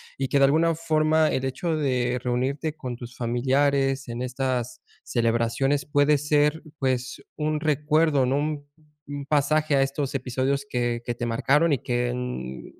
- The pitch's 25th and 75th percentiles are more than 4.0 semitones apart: No, average, 3.1 semitones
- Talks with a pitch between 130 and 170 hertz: Yes, low, 135 Hz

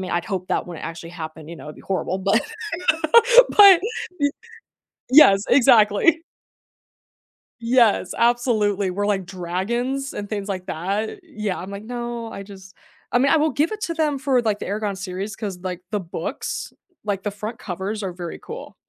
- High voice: Yes, high, 205 Hz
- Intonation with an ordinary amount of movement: Yes, average, 4.3 semitones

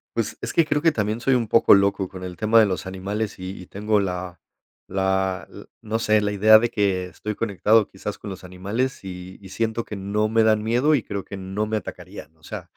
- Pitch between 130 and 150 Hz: No, low, 105 Hz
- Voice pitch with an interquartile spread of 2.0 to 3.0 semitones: Yes, average, 2.7 semitones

